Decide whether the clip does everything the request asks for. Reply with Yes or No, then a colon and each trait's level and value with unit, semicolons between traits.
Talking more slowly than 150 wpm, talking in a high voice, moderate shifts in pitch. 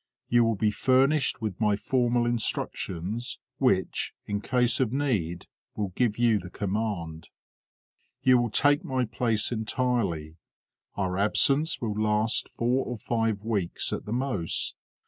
No: average, 140 wpm; low, 115 Hz; average, 3.3 semitones